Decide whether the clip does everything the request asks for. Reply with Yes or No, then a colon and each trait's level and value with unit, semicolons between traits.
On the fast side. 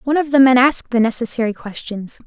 Yes: fast, 210 wpm